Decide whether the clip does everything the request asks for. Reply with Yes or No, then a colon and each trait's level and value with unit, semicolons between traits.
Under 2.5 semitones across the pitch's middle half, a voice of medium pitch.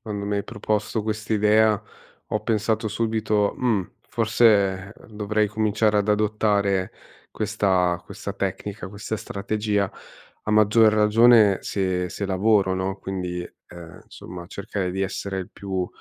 No: narrow, 2.1 semitones; low, 105 Hz